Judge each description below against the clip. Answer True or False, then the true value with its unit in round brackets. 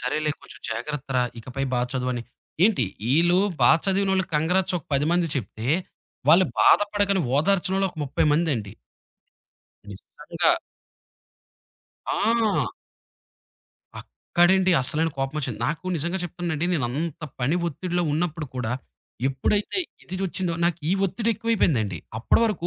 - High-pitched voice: False (165 Hz)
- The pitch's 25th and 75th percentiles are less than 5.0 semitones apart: False (5.6 semitones)